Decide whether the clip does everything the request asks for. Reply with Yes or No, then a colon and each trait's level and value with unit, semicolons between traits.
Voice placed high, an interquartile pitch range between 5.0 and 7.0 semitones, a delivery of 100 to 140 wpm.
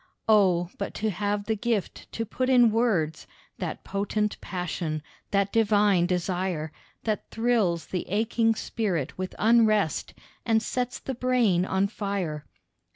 No: high, 205 Hz; average, 3.8 semitones; slow, 135 wpm